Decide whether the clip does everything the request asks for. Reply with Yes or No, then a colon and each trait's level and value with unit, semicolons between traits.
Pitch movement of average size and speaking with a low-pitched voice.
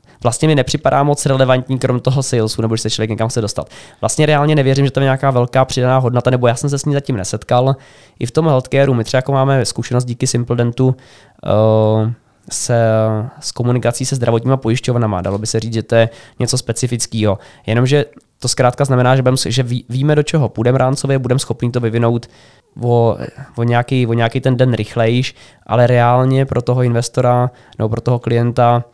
No: narrow, 2.3 semitones; low, 125 Hz